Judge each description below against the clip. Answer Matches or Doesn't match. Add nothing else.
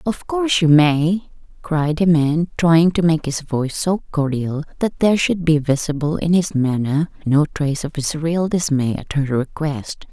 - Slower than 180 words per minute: Doesn't match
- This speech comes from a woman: Matches